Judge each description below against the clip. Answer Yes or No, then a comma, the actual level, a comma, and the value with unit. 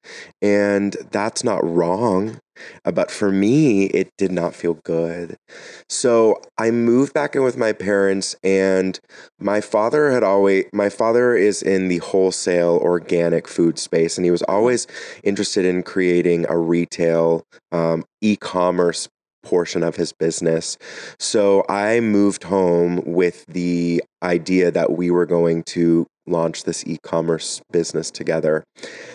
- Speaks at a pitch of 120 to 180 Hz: No, very low, 90 Hz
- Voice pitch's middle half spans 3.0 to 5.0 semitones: No, narrow, 2.6 semitones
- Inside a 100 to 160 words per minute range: Yes, slow, 135 wpm